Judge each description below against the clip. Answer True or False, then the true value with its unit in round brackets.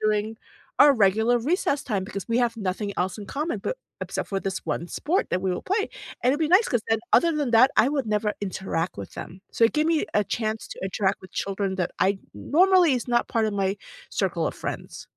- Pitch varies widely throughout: True (6.2 semitones)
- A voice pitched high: True (220 Hz)